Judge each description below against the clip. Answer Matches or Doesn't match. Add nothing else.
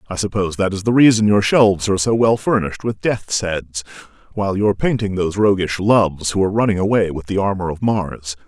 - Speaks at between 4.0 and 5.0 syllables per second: Doesn't match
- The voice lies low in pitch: Matches